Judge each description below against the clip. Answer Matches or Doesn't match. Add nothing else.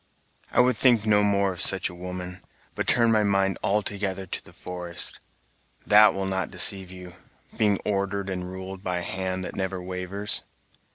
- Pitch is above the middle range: Doesn't match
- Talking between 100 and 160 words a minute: Doesn't match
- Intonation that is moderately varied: Doesn't match